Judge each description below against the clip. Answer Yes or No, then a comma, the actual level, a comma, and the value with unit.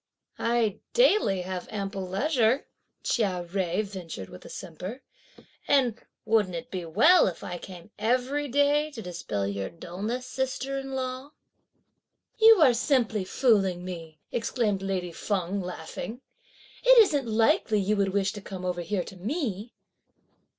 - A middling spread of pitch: No, wide, 5.9 semitones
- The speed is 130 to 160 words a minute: Yes, average, 145 wpm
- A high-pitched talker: Yes, high, 210 Hz